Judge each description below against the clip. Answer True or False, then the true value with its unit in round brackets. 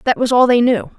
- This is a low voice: False (235 Hz)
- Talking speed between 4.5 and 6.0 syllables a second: True (5.8 syllables/s)